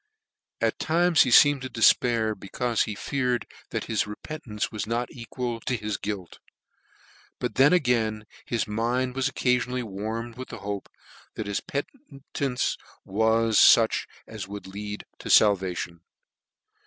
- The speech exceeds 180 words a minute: No, average, 140 wpm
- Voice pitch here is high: No, low, 115 Hz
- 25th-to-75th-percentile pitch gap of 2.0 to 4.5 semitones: Yes, average, 3.3 semitones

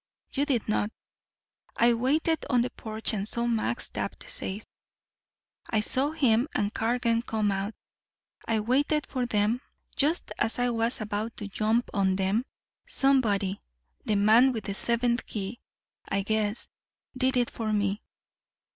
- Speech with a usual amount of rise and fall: Yes, average, 3.0 semitones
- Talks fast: No, average, 150 wpm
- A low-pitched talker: No, high, 225 Hz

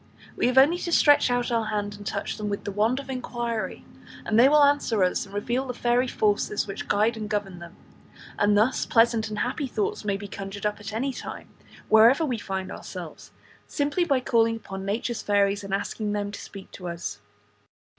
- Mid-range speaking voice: No, high, 220 Hz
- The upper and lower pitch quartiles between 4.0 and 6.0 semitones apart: No, average, 3.6 semitones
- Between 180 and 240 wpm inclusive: Yes, fast, 205 wpm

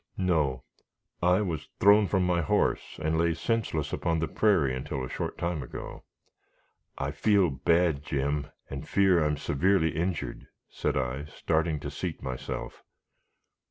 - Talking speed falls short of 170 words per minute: Yes, average, 150 wpm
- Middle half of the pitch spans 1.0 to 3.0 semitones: No, average, 4.1 semitones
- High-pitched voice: No, very low, 80 Hz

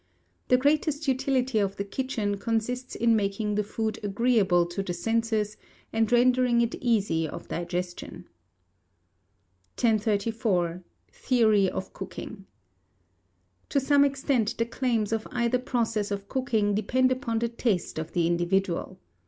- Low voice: No, high, 220 Hz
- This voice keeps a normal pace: No, slow, 130 wpm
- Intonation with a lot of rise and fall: No, average, 3.8 semitones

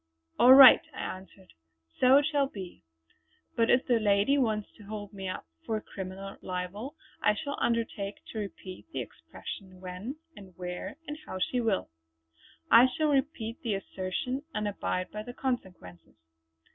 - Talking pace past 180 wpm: No, average, 160 wpm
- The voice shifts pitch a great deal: No, average, 5.0 semitones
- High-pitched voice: Yes, high, 210 Hz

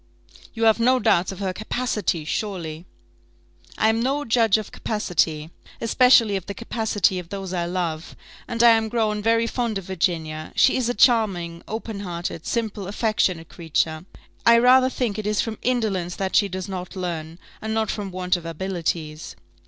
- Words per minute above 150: Yes, average, 175 wpm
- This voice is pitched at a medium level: No, high, 200 Hz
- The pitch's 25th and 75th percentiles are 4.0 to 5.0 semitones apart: Yes, average, 4.4 semitones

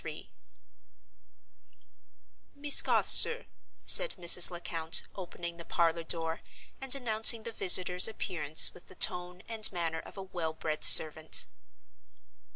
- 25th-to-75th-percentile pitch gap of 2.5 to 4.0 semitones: No, average, 4.8 semitones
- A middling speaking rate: No, slow, 120 wpm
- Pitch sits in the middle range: Yes, medium, 180 Hz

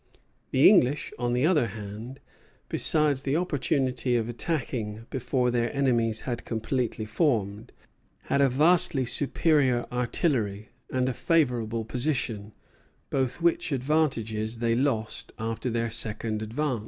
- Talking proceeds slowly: Yes, slow, 125 wpm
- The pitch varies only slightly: No, average, 3.6 semitones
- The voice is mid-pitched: No, low, 125 Hz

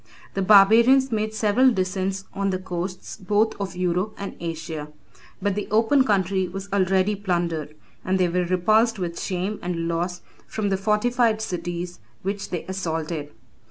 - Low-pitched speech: No, high, 190 Hz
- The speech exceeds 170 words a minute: No, average, 155 wpm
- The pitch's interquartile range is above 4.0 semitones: No, average, 3.0 semitones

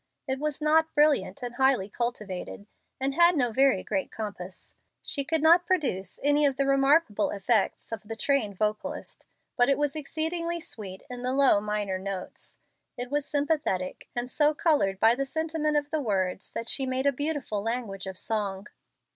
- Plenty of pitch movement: Yes, wide, 6.1 semitones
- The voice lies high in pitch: Yes, very high, 260 Hz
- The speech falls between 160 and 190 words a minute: Yes, average, 175 wpm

